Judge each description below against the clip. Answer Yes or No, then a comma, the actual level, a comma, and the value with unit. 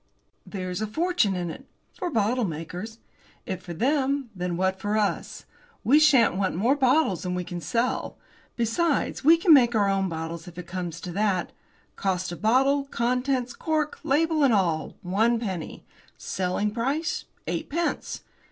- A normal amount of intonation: No, wide, 7.0 semitones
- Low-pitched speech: No, high, 215 Hz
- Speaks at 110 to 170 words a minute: Yes, average, 160 wpm